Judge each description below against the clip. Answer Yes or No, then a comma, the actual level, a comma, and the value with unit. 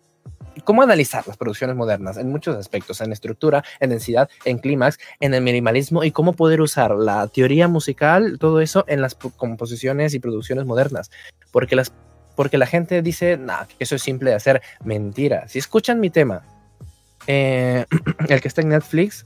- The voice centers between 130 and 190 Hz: Yes, low, 135 Hz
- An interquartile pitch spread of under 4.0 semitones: No, average, 4.6 semitones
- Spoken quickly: No, average, 175 wpm